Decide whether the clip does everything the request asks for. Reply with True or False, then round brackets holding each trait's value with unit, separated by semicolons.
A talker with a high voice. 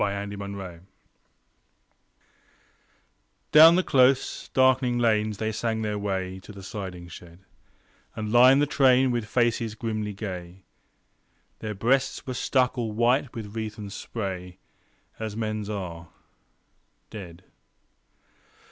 False (110 Hz)